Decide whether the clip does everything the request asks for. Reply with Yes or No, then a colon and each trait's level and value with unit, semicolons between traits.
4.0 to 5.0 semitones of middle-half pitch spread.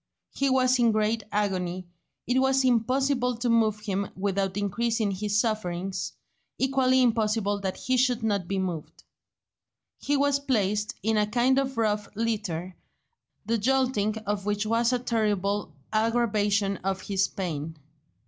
No: average, 3.6 semitones